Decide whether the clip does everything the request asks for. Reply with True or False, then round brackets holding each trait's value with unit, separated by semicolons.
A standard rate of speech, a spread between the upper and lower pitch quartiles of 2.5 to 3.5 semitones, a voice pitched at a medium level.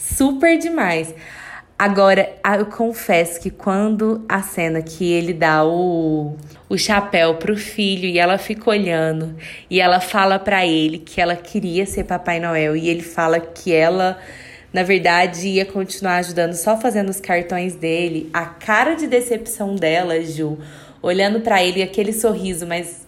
True (155 wpm; 3.2 semitones; 180 Hz)